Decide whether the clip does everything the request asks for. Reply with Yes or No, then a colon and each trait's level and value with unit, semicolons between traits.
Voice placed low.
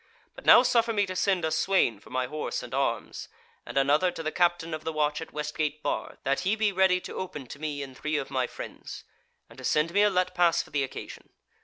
No: medium, 155 Hz